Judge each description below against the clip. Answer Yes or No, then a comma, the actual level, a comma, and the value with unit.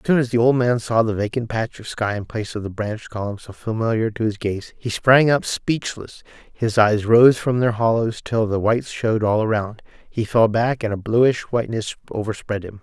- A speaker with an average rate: No, fast, 225 wpm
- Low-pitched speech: Yes, low, 110 Hz